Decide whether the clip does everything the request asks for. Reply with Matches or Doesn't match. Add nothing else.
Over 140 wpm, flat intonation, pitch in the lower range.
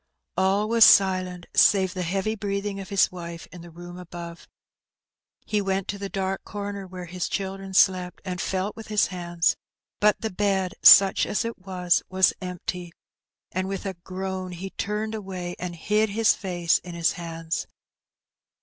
Doesn't match